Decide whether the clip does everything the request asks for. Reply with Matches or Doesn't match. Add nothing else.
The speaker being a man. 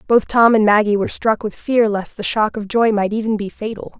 Doesn't match